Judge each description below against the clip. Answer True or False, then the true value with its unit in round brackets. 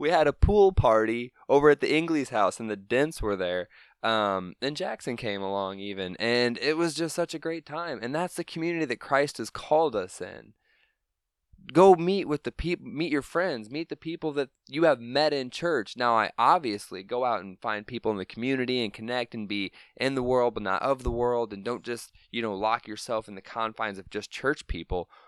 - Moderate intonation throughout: False (6.1 semitones)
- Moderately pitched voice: False (120 Hz)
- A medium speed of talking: False (220 wpm)